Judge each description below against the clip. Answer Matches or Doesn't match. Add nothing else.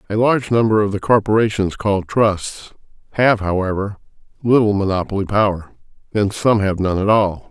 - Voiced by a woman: Doesn't match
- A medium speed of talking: Matches